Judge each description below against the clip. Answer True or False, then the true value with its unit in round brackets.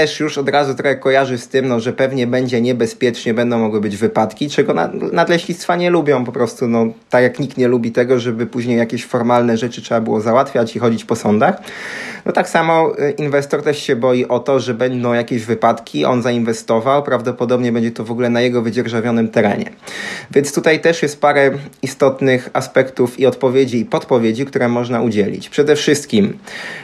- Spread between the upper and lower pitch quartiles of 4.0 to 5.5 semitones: False (3.1 semitones)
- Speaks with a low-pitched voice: True (125 Hz)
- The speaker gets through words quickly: True (185 wpm)